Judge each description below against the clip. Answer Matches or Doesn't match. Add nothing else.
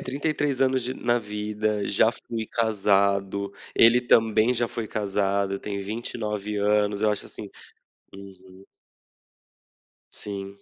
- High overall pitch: Doesn't match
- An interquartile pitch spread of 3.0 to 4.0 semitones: Doesn't match